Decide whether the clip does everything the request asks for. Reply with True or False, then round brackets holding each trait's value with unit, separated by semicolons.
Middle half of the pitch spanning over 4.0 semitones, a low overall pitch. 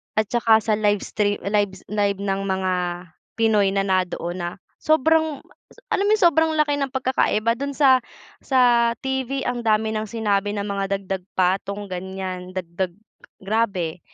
False (4.7 semitones; 210 Hz)